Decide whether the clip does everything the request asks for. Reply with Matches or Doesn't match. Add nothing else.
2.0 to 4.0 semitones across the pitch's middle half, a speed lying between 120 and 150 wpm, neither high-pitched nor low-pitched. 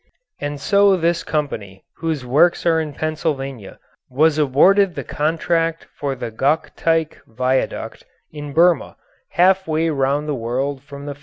Matches